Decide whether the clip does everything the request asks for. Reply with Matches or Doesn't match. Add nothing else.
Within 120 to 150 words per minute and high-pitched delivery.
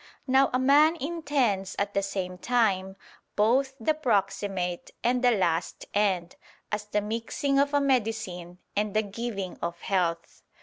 Matches